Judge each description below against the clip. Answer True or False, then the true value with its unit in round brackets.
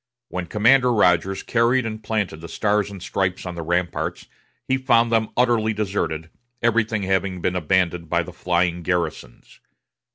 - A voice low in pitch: True (95 Hz)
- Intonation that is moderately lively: True (4.2 semitones)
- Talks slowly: False (155 wpm)